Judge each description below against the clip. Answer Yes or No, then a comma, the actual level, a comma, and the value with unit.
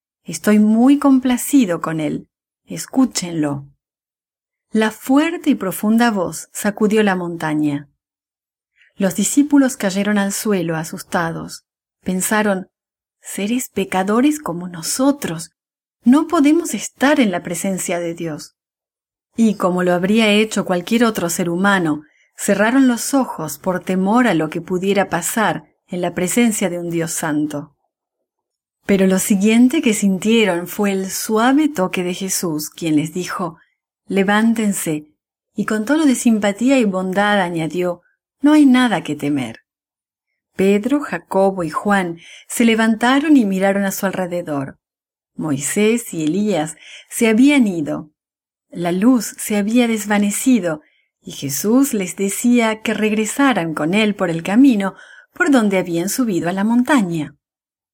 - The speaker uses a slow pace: Yes, slow, 130 wpm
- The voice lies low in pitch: No, high, 195 Hz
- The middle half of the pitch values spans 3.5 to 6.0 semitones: Yes, average, 5.1 semitones